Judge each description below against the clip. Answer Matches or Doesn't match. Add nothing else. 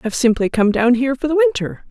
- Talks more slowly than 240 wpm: Doesn't match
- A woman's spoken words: Matches